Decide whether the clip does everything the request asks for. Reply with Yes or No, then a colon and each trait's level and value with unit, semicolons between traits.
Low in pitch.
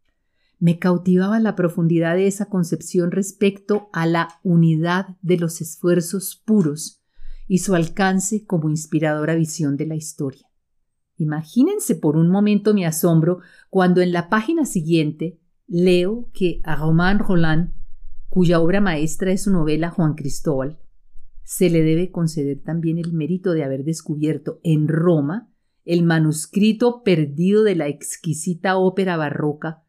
No: medium, 170 Hz